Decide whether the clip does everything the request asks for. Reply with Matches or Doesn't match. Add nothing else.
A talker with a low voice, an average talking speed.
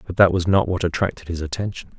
Doesn't match